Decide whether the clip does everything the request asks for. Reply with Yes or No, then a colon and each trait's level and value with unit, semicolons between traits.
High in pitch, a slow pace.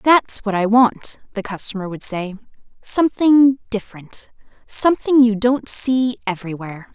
Yes: high, 225 Hz; slow, 110 wpm